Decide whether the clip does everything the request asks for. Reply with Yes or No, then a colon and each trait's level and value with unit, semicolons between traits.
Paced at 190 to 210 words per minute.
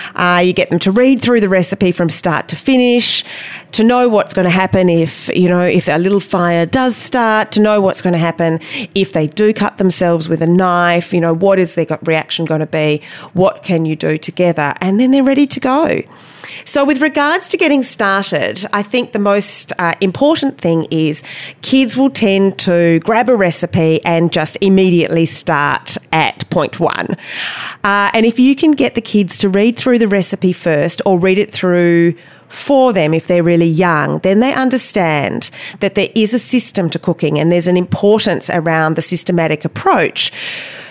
Yes: average, 195 wpm